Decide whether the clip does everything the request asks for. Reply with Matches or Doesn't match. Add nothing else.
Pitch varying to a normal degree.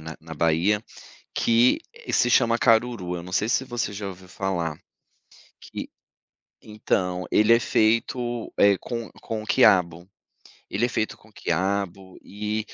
Matches